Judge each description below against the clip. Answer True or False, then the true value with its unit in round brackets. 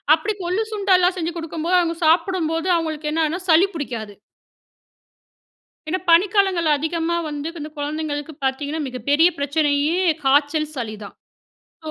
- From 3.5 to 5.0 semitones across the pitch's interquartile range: False (2.9 semitones)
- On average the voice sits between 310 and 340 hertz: True (315 Hz)